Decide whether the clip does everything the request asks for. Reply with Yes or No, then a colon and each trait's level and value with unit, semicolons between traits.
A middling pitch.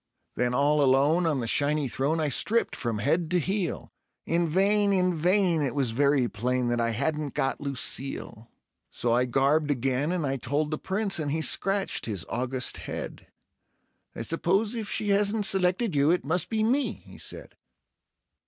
Yes: medium, 150 Hz